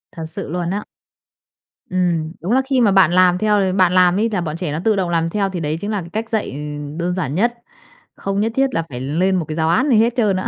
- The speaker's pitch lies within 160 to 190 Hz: Yes, medium, 185 Hz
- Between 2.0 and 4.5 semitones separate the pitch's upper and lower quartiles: Yes, average, 4.0 semitones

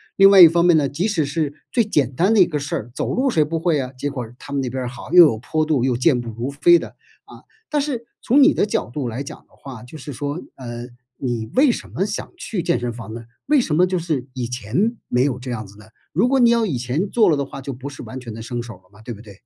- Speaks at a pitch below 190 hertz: Yes, medium, 140 Hz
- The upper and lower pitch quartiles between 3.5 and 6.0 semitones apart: No, wide, 6.6 semitones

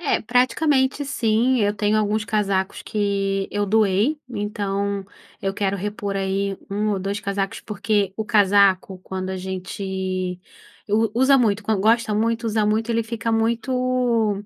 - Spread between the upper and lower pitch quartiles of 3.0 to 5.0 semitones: No, narrow, 2.5 semitones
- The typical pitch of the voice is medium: No, high, 210 Hz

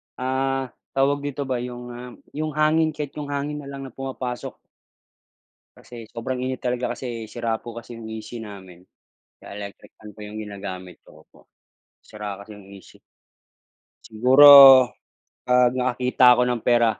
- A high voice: No, low, 125 Hz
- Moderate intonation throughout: Yes, average, 3.5 semitones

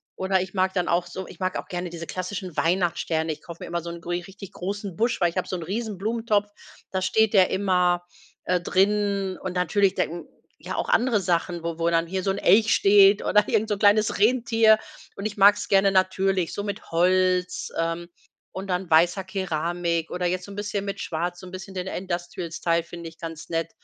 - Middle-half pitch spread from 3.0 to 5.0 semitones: No, narrow, 2.5 semitones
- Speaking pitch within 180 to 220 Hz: Yes, medium, 185 Hz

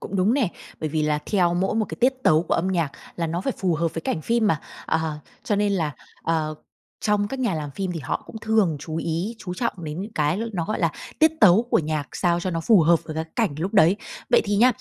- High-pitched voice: No, medium, 175 Hz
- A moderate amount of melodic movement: Yes, average, 4.6 semitones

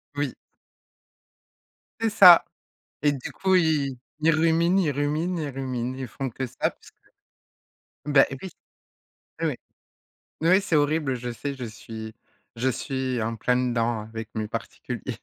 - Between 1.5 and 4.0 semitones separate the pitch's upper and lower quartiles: No, average, 4.7 semitones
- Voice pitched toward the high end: No, low, 135 Hz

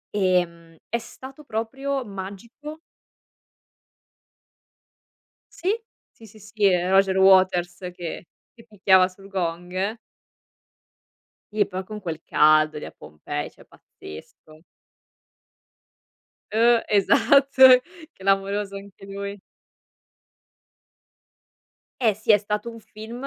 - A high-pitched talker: Yes, high, 200 Hz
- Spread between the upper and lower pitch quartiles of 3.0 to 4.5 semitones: Yes, average, 3.4 semitones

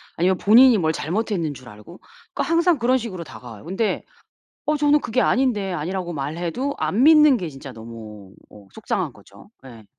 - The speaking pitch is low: No, medium, 185 Hz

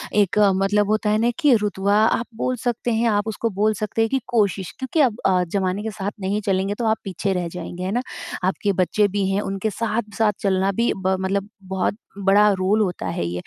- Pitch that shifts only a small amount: Yes, narrow, 2.3 semitones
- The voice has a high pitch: Yes, high, 205 Hz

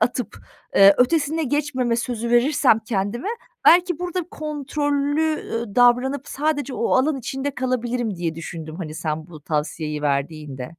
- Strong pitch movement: Yes, wide, 8.8 semitones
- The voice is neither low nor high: No, high, 245 Hz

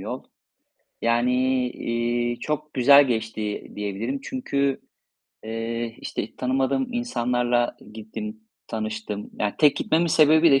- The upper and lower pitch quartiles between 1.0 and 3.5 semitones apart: No, average, 4.8 semitones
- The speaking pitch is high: No, low, 120 Hz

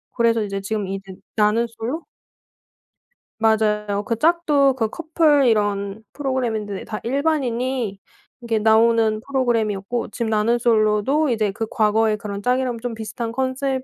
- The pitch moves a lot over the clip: No, average, 3.5 semitones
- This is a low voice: No, high, 225 Hz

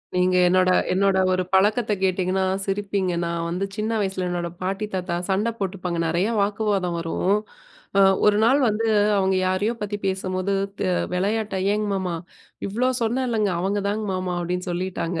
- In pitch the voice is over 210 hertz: No, high, 190 Hz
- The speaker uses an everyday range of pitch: No, narrow, 2.3 semitones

